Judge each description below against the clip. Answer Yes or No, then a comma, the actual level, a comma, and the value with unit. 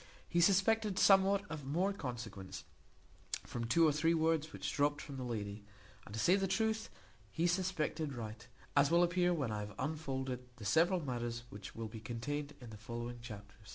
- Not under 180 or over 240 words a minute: Yes, average, 185 wpm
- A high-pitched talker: No, medium, 145 Hz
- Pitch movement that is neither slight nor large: No, wide, 6.7 semitones